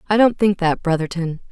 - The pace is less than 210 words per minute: Yes, average, 200 wpm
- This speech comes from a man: No, female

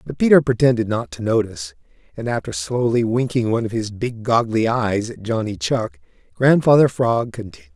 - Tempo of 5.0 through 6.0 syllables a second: Yes, 5.4 syllables/s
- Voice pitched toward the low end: Yes, low, 115 Hz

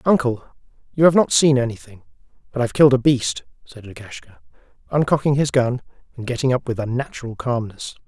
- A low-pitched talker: Yes, low, 125 Hz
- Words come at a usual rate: Yes, average, 165 wpm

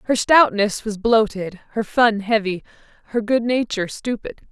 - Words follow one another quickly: No, average, 145 wpm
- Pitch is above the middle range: Yes, high, 220 Hz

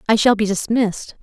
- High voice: Yes, high, 215 Hz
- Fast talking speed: No, average, 195 wpm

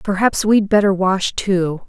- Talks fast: No, average, 160 wpm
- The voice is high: Yes, high, 195 Hz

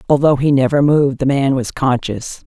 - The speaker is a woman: Yes, female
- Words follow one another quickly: No, average, 190 wpm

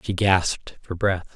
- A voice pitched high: No, very low, 95 Hz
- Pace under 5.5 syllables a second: Yes, 4.2 syllables/s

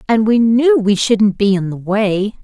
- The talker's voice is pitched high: Yes, high, 215 Hz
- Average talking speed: No, fast, 220 wpm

